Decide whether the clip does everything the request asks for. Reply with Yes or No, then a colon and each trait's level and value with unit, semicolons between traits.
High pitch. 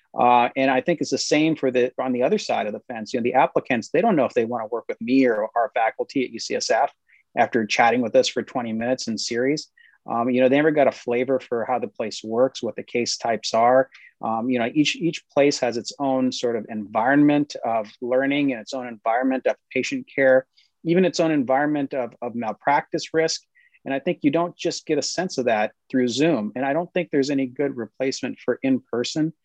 No: low, 135 Hz